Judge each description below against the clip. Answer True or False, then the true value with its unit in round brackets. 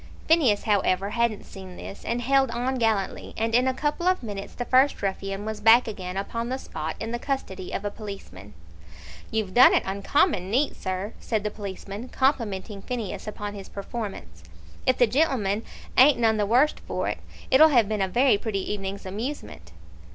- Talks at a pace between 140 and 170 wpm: False (180 wpm)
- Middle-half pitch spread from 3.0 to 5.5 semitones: True (4.2 semitones)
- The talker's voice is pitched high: True (215 Hz)